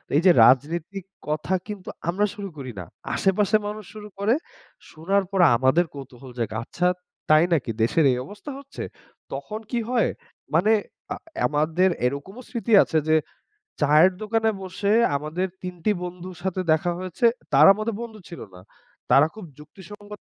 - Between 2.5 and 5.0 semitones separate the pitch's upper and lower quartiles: No, wide, 5.4 semitones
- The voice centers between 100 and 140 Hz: No, medium, 180 Hz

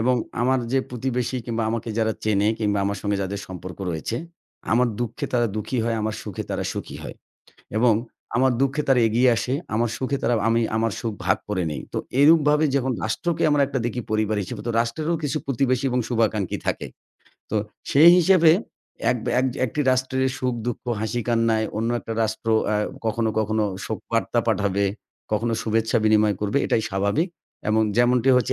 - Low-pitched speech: Yes, low, 115 Hz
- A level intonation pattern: No, average, 3.0 semitones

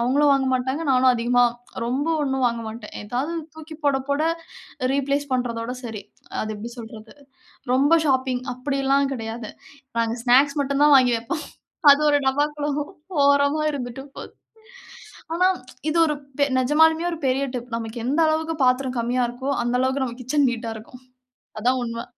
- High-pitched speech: Yes, very high, 260 Hz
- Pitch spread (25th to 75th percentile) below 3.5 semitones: Yes, average, 3.1 semitones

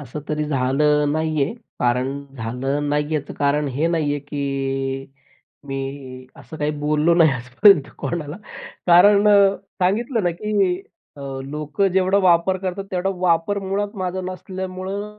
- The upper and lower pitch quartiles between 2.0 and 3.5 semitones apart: No, average, 4.9 semitones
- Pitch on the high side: No, medium, 155 Hz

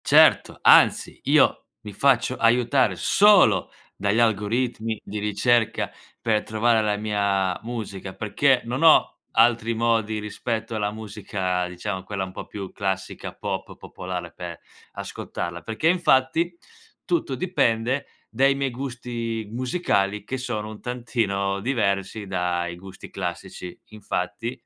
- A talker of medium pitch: No, low, 110 Hz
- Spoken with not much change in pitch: No, average, 3.8 semitones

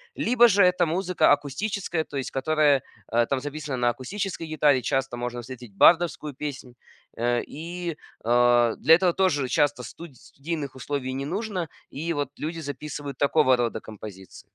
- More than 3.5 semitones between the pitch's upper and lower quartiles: Yes, average, 4.8 semitones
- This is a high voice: No, medium, 145 Hz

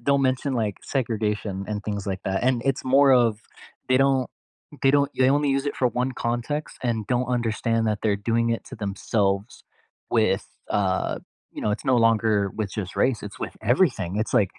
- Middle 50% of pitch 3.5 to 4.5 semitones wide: Yes, average, 3.9 semitones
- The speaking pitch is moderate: No, low, 115 Hz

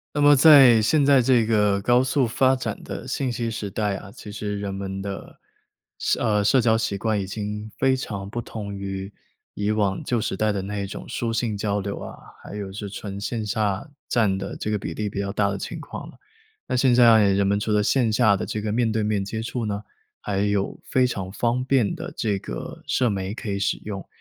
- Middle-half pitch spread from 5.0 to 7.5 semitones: No, average, 3.0 semitones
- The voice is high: No, low, 105 Hz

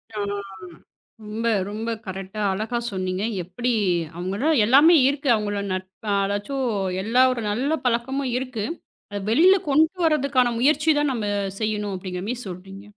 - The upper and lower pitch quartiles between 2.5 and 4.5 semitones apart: No, average, 5.2 semitones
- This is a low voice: No, high, 225 Hz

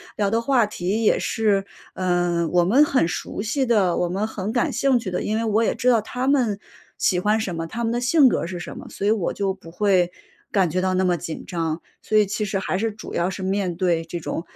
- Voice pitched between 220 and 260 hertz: No, high, 195 Hz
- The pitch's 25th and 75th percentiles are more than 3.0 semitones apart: Yes, average, 3.9 semitones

